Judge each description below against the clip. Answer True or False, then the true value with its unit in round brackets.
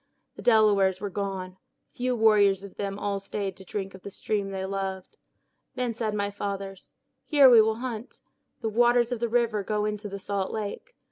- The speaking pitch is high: True (205 Hz)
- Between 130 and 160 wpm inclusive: False (190 wpm)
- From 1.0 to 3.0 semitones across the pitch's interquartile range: True (2.4 semitones)